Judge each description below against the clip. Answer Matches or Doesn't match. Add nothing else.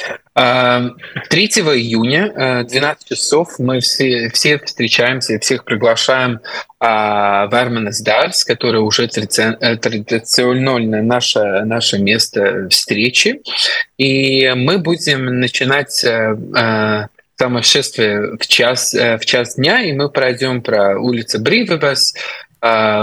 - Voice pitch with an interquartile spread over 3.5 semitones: Doesn't match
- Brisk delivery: Doesn't match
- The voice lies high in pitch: Doesn't match